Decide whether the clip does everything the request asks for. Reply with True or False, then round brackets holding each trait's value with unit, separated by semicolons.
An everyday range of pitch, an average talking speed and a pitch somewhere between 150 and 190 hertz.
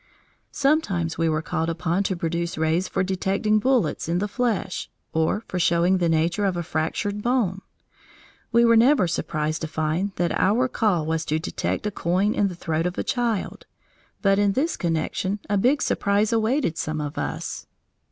True (4.4 semitones; 180 wpm; 185 Hz)